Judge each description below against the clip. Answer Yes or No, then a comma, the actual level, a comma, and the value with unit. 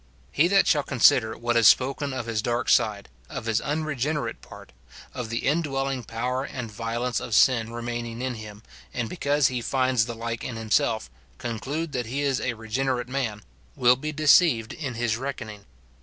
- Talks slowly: No, average, 175 wpm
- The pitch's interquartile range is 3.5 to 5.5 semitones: No, average, 3.1 semitones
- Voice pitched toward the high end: No, low, 125 Hz